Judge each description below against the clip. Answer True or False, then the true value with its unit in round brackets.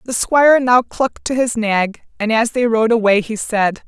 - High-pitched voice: True (230 Hz)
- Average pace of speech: False (215 wpm)